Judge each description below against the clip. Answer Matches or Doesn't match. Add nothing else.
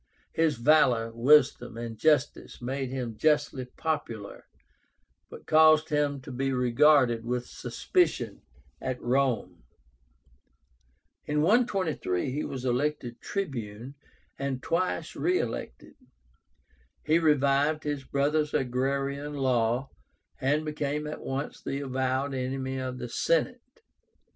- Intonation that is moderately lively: Matches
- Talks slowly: Matches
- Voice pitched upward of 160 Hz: Doesn't match